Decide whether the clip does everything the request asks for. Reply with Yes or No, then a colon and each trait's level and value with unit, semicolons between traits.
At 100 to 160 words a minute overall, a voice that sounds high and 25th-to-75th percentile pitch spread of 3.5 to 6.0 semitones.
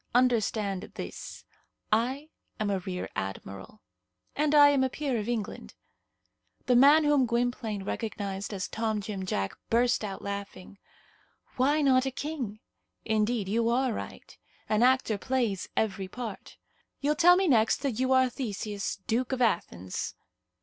Yes: average, 145 wpm; high, 230 Hz; average, 4.5 semitones